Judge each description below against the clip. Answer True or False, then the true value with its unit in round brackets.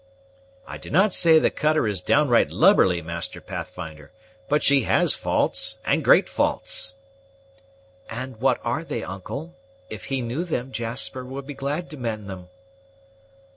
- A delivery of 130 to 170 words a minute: True (155 wpm)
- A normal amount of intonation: False (5.7 semitones)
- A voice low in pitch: True (125 Hz)